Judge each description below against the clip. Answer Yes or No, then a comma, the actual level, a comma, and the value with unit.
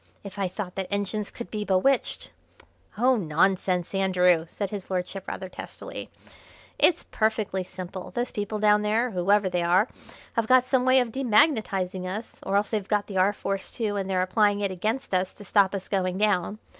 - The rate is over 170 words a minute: Yes, average, 190 wpm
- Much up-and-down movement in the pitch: No, narrow, 2.5 semitones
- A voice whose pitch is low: No, high, 200 Hz